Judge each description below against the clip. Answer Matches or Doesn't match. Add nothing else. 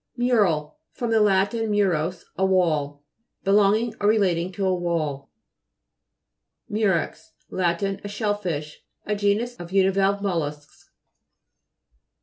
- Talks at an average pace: Doesn't match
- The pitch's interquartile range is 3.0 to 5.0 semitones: Matches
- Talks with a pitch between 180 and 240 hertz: Matches